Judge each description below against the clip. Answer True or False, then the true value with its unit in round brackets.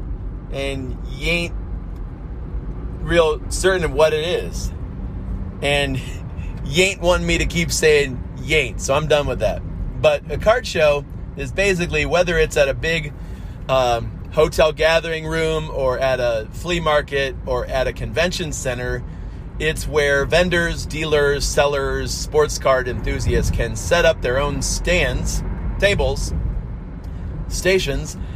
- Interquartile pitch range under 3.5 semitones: False (5.4 semitones)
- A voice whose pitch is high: False (145 Hz)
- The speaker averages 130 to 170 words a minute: True (140 wpm)